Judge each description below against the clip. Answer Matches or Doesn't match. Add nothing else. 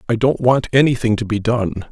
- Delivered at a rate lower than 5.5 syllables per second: Doesn't match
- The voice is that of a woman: Doesn't match